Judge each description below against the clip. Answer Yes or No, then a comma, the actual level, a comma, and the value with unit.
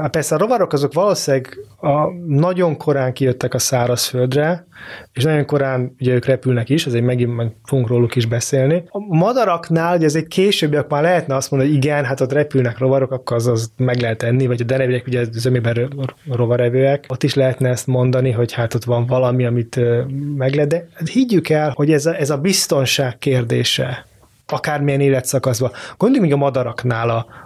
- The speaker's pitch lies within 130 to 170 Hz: Yes, low, 135 Hz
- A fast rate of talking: Yes, fast, 185 wpm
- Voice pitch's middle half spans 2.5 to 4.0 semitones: Yes, average, 3.3 semitones